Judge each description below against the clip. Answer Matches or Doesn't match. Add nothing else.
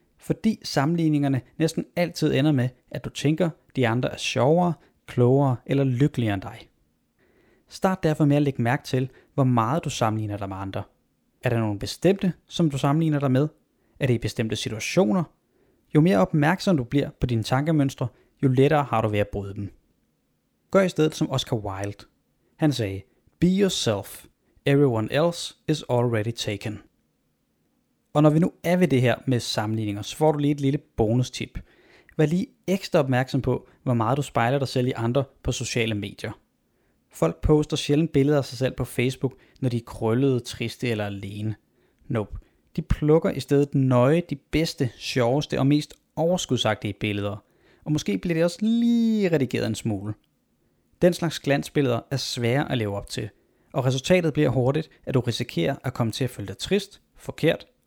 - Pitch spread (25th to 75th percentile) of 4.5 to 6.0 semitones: Matches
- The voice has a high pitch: Doesn't match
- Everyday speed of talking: Matches